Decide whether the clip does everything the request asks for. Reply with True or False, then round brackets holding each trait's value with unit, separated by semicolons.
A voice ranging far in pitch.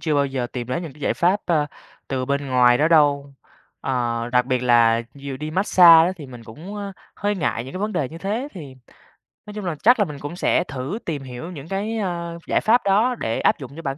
True (6.2 semitones)